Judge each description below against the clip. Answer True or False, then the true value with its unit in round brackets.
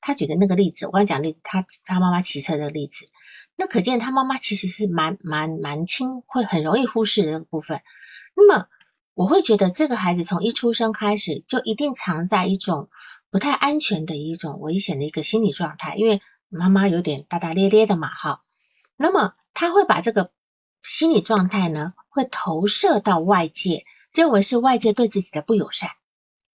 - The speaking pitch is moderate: False (200 Hz)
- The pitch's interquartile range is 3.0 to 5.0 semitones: False (5.5 semitones)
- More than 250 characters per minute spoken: True (290 characters per minute)